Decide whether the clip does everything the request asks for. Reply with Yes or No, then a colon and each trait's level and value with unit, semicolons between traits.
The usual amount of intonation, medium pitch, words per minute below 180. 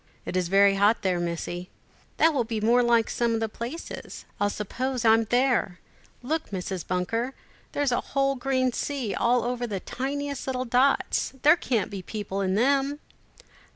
No: average, 4.8 semitones; high, 235 Hz; average, 170 wpm